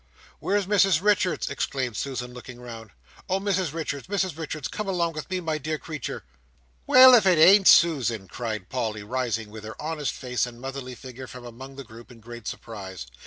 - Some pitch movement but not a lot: No, wide, 6.3 semitones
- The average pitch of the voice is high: No, low, 135 Hz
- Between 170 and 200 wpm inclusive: Yes, average, 190 wpm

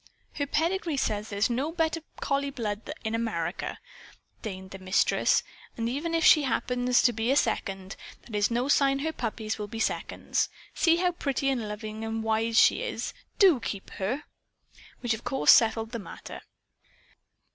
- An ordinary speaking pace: Yes, average, 165 wpm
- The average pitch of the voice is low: No, high, 230 Hz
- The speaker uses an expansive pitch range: No, average, 4.6 semitones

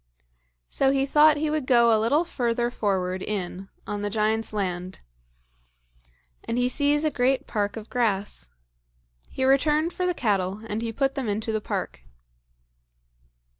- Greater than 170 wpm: No, average, 155 wpm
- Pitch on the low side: No, high, 230 Hz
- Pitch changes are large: No, average, 4.8 semitones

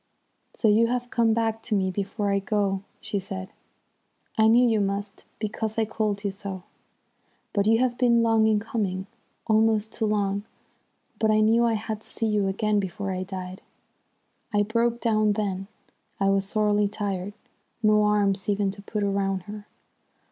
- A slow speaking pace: No, average, 170 wpm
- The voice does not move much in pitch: Yes, narrow, 1.9 semitones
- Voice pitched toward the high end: Yes, high, 210 Hz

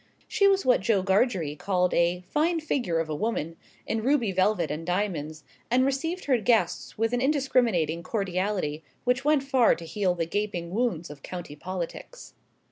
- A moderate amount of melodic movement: No, wide, 6.7 semitones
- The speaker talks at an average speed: Yes, average, 170 wpm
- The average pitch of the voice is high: Yes, high, 200 Hz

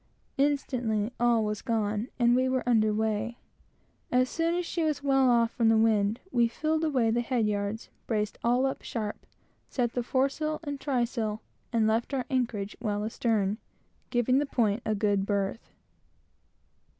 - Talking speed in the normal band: Yes, average, 160 wpm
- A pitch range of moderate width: Yes, average, 3.2 semitones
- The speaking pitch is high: Yes, high, 235 Hz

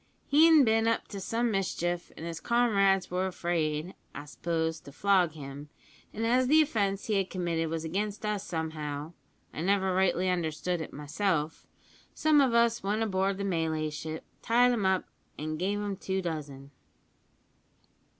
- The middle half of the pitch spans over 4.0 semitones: Yes, average, 4.6 semitones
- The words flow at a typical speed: Yes, average, 160 wpm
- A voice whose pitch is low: No, medium, 185 Hz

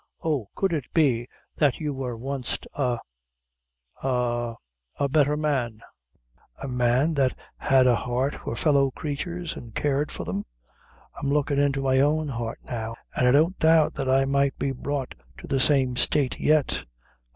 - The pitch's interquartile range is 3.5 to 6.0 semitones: No, average, 2.9 semitones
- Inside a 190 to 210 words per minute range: No, average, 160 wpm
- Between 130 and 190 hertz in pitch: Yes, low, 135 Hz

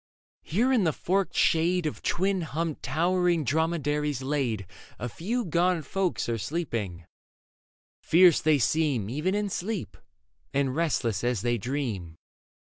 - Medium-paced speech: No, slow, 130 wpm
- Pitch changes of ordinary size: No, wide, 6.0 semitones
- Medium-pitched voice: Yes, medium, 155 Hz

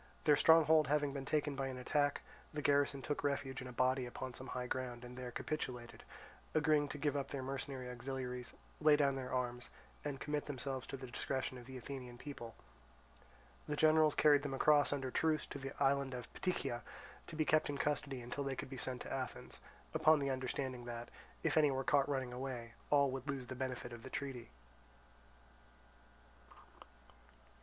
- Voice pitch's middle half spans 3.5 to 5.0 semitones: No, narrow, 2.4 semitones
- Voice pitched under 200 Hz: Yes, low, 135 Hz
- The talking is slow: No, average, 185 wpm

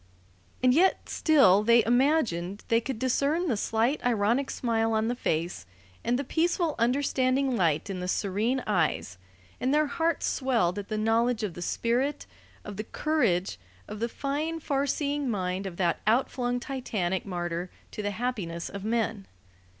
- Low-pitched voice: No, high, 230 Hz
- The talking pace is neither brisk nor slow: Yes, average, 160 wpm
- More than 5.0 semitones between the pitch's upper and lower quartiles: Yes, wide, 5.5 semitones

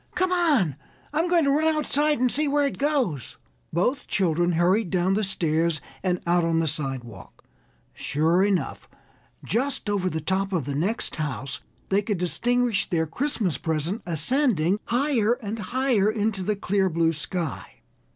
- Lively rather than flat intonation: Yes, wide, 7.0 semitones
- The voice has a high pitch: Yes, high, 195 Hz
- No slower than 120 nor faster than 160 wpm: Yes, average, 155 wpm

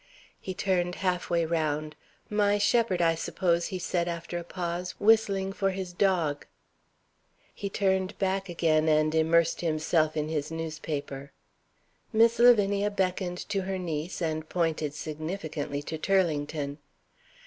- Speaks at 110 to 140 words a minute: Yes, slow, 135 wpm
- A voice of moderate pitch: Yes, medium, 175 Hz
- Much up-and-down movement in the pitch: No, average, 3.5 semitones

